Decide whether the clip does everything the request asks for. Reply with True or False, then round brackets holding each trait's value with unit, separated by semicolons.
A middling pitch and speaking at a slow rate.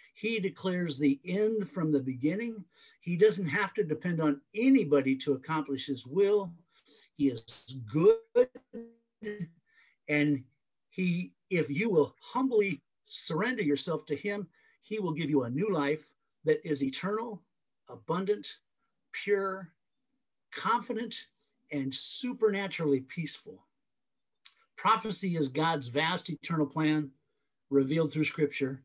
True (165 Hz; 115 wpm)